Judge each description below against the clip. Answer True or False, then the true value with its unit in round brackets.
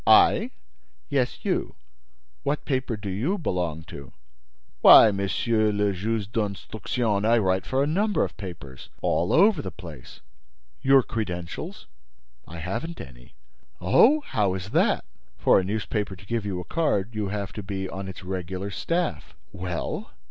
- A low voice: True (100 Hz)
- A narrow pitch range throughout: False (4.4 semitones)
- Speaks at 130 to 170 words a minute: True (150 wpm)